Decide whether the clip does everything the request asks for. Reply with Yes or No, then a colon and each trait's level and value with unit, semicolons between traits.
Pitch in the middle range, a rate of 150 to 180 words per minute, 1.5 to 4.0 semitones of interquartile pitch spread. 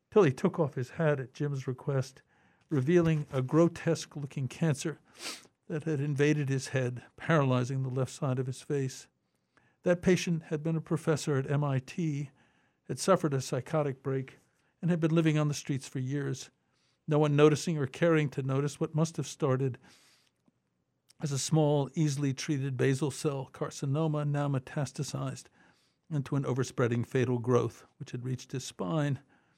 Yes: medium, 145 Hz; average, 160 wpm; average, 2.9 semitones